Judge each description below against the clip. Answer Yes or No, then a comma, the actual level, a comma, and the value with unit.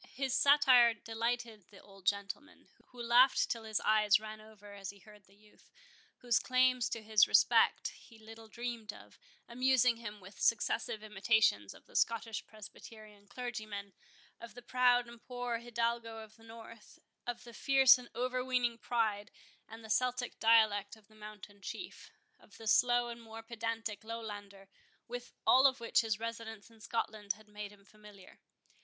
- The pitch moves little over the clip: Yes, narrow, 2.3 semitones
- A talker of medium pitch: No, high, 225 Hz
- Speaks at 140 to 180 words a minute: Yes, average, 165 wpm